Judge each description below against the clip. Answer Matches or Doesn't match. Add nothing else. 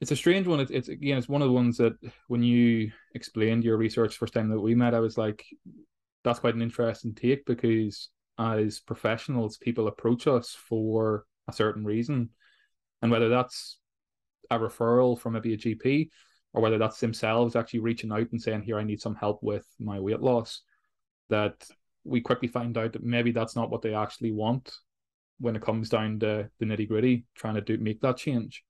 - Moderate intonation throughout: Doesn't match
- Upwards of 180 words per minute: Matches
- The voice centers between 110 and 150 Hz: Matches